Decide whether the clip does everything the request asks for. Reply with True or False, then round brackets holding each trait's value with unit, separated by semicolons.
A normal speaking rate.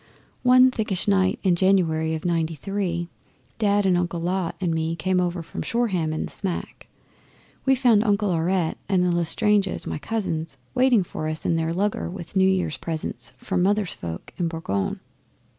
True (175 wpm)